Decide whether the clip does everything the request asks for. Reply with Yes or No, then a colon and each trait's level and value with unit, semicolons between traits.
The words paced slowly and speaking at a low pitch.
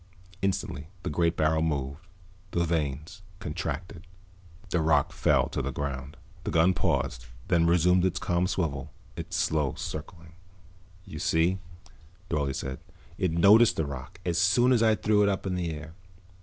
No: average, 155 wpm; very low, 85 Hz